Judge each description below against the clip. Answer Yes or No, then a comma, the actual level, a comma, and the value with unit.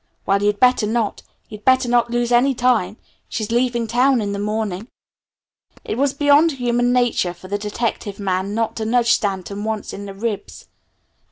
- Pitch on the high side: Yes, high, 225 Hz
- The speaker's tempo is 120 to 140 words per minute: No, average, 175 wpm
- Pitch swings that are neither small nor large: Yes, average, 3.2 semitones